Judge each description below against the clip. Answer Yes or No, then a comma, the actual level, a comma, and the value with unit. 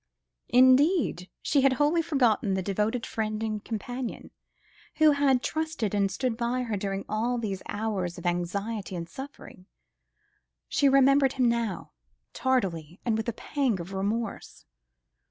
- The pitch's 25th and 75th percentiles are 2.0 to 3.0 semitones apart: No, average, 4.8 semitones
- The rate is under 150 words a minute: Yes, average, 140 wpm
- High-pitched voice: Yes, high, 225 Hz